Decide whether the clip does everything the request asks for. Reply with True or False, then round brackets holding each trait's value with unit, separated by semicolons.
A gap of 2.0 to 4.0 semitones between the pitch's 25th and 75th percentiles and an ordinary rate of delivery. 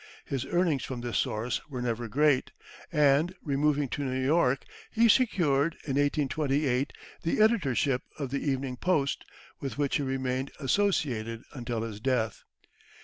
True (3.1 semitones; 145 wpm)